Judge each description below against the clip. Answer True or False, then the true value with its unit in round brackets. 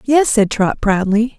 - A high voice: True (225 Hz)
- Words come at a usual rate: True (175 wpm)